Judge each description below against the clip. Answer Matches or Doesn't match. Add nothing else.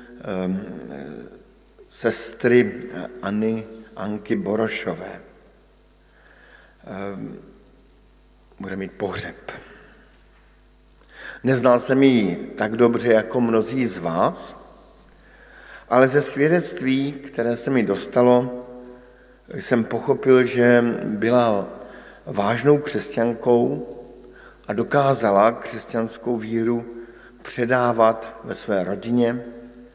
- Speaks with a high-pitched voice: Doesn't match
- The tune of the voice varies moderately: Doesn't match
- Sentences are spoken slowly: Matches